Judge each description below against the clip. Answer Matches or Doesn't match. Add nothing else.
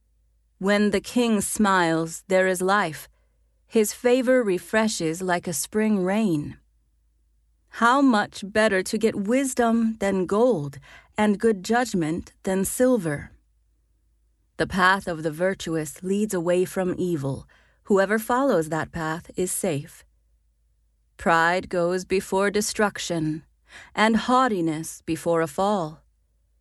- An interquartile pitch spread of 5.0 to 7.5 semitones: Matches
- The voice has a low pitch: Doesn't match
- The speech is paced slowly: Matches